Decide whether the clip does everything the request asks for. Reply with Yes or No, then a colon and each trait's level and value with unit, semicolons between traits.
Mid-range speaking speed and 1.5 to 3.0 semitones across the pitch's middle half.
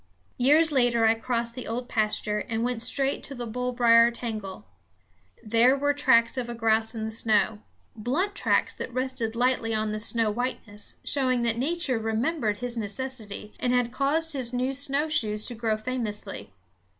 Yes: average, 165 wpm; average, 2.7 semitones